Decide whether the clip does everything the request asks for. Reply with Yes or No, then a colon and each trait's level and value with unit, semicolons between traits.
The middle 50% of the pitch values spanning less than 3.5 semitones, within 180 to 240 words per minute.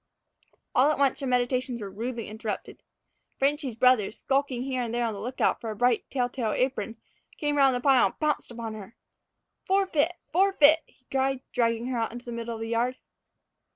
Yes: average, 2.8 semitones; average, 190 wpm